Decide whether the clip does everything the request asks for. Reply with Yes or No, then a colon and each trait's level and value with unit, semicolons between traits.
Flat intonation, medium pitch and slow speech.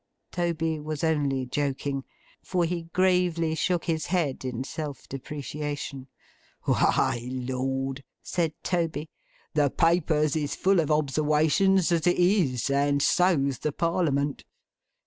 No: average, 3.4 semitones; medium, 150 Hz; slow, 120 wpm